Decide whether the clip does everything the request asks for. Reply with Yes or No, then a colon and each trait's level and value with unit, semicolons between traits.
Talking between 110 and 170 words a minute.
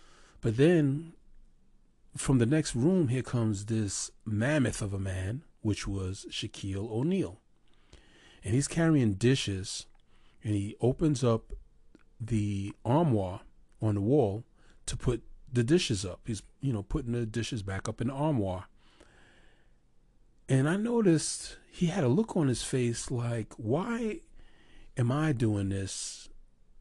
Yes: average, 140 wpm